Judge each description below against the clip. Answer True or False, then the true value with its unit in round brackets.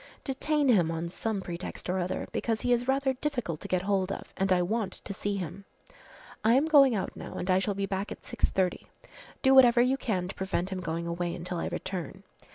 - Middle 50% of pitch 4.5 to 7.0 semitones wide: True (5.2 semitones)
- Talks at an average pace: False (220 wpm)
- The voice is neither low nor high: False (195 Hz)